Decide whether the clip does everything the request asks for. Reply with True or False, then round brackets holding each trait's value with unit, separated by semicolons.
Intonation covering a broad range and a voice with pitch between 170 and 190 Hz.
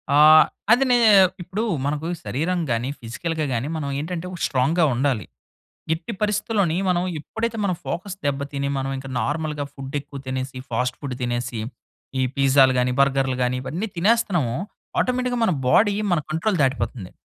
False (5.7 semitones; 145 Hz)